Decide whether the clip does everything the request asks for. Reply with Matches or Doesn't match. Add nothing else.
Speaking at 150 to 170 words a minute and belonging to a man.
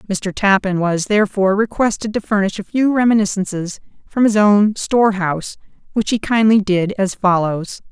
Doesn't match